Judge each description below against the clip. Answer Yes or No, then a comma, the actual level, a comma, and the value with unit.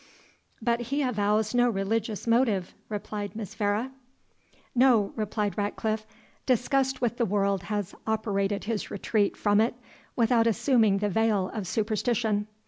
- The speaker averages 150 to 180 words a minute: No, slow, 135 wpm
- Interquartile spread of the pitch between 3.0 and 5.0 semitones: No, narrow, 2.4 semitones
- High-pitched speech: Yes, high, 215 Hz